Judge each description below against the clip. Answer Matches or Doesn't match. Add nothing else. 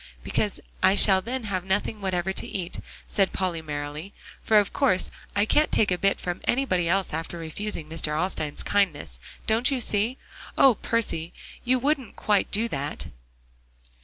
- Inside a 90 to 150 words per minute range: Doesn't match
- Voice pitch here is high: Matches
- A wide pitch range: Doesn't match